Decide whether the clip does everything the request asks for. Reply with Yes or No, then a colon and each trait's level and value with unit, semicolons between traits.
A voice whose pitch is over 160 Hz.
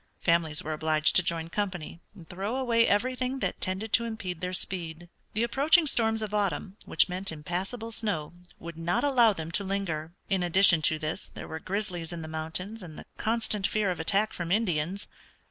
Yes: medium, 185 Hz